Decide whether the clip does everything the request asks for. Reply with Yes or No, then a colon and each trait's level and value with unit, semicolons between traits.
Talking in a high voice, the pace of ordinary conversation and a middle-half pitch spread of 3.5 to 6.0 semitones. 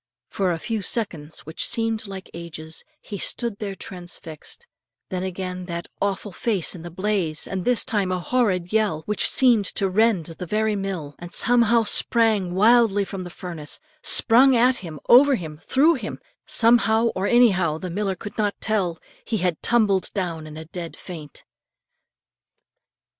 Yes: high, 195 Hz; average, 165 wpm; average, 4.3 semitones